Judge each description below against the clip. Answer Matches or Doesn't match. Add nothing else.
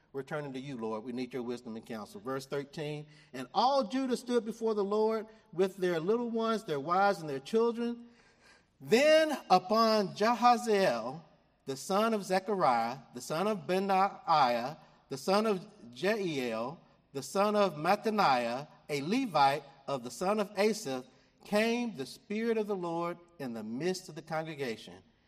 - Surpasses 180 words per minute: Doesn't match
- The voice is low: Doesn't match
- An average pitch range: Doesn't match